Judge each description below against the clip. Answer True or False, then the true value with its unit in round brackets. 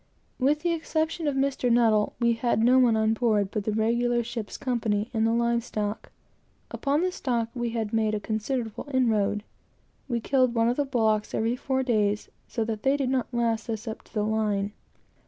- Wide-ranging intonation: False (2.8 semitones)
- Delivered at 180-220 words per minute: True (190 wpm)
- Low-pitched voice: False (230 Hz)